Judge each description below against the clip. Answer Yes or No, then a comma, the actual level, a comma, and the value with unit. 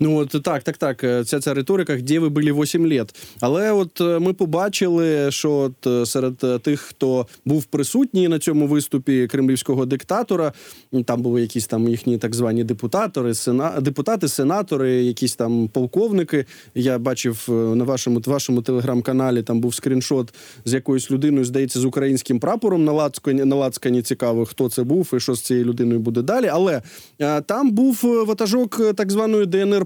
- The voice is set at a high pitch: No, low, 135 Hz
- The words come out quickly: Yes, fast, 165 wpm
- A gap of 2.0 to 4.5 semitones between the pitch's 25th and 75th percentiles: Yes, average, 4.2 semitones